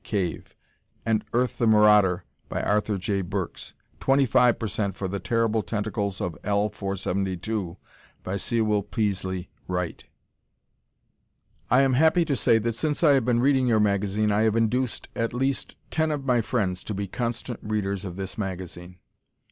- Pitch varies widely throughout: No, average, 3.6 semitones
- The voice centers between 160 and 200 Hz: No, low, 105 Hz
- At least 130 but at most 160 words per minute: Yes, average, 155 wpm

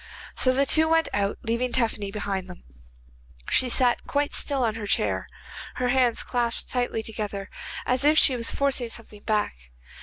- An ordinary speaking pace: Yes, average, 170 wpm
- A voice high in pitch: Yes, high, 240 Hz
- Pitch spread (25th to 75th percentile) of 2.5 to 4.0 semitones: Yes, average, 3.5 semitones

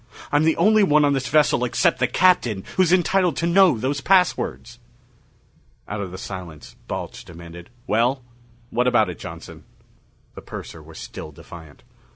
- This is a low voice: Yes, low, 125 Hz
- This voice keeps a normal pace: Yes, average, 160 wpm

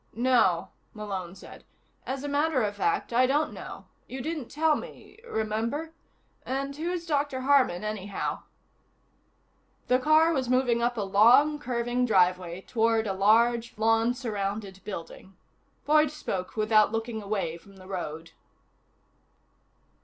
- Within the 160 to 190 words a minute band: No, slow, 135 wpm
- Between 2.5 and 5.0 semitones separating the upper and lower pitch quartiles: No, wide, 5.5 semitones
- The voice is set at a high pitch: Yes, high, 230 Hz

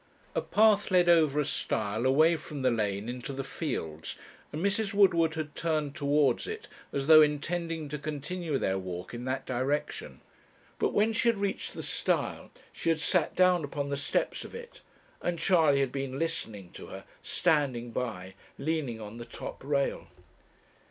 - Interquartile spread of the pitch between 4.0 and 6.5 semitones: Yes, average, 4.8 semitones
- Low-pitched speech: No, medium, 150 Hz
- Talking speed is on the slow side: No, average, 170 wpm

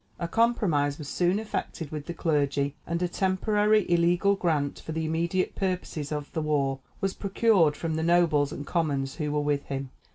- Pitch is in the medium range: Yes, medium, 160 Hz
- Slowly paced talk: No, average, 185 wpm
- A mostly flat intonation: No, average, 3.8 semitones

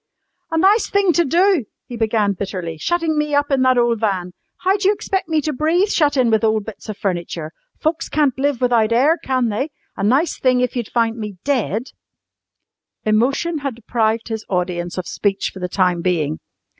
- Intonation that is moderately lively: No, wide, 6.6 semitones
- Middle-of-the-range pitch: No, high, 240 Hz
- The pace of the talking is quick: No, average, 195 wpm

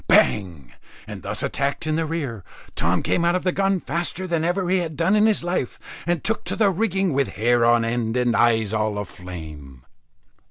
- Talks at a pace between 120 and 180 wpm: No, average, 200 wpm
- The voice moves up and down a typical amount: No, wide, 8.2 semitones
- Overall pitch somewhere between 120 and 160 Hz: Yes, medium, 140 Hz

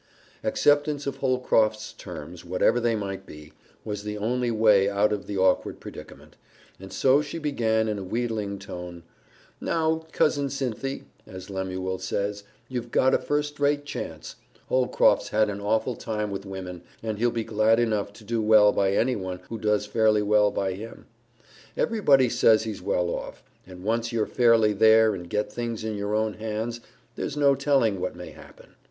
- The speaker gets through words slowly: No, average, 170 wpm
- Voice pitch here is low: Yes, low, 110 Hz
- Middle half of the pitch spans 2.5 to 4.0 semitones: Yes, average, 3.3 semitones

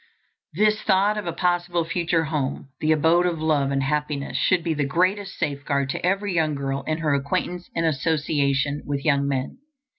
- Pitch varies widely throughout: No, average, 3.8 semitones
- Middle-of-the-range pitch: Yes, medium, 155 Hz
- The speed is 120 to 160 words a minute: No, average, 180 wpm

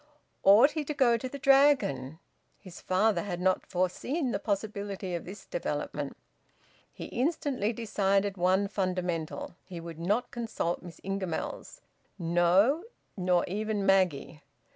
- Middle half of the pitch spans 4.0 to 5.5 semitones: Yes, average, 4.7 semitones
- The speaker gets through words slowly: Yes, slow, 130 wpm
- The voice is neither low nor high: No, high, 195 Hz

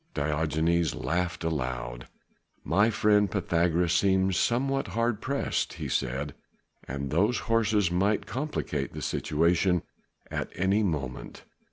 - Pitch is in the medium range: No, very low, 90 Hz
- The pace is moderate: No, slow, 115 wpm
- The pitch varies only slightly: No, average, 5.2 semitones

